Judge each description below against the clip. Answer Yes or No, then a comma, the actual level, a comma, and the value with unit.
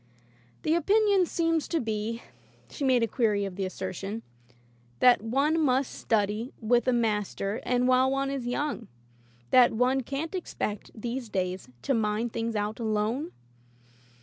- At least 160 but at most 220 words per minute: No, average, 150 wpm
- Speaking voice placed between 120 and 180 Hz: No, high, 240 Hz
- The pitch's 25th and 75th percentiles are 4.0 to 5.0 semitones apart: Yes, average, 4.3 semitones